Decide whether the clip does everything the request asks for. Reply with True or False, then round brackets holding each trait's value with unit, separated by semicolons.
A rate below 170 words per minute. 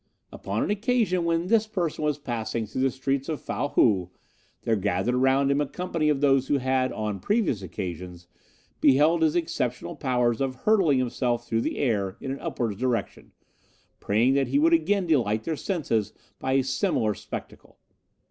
False (175 wpm)